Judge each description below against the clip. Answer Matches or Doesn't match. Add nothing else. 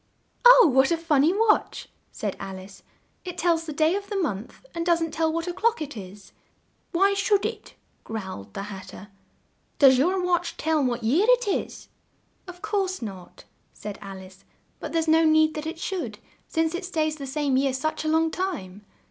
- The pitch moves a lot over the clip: Matches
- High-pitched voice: Matches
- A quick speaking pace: Doesn't match